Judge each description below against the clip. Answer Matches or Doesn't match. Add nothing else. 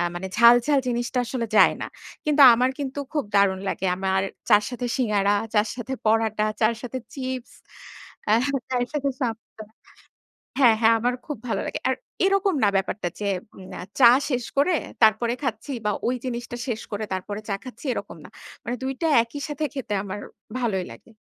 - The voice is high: Matches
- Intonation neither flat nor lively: Matches